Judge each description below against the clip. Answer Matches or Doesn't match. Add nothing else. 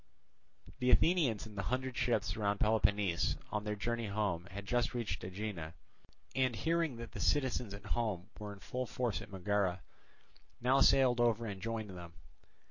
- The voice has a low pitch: Matches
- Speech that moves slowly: Doesn't match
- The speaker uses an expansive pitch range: Doesn't match